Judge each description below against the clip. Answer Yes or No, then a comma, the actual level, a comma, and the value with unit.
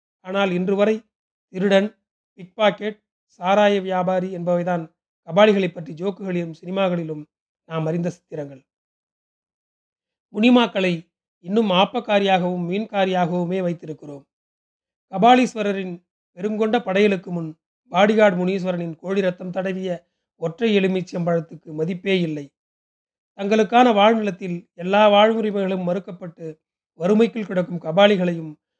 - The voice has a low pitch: No, medium, 185 Hz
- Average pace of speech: Yes, average, 85 wpm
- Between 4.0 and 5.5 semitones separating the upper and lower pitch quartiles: No, average, 2.8 semitones